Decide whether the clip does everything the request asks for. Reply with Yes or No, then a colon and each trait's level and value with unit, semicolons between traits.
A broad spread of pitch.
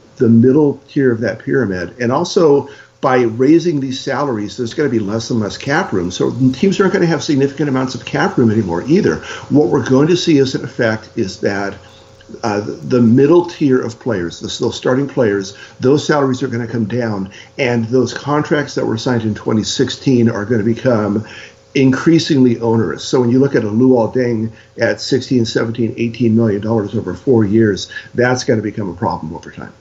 No: average, 3.6 semitones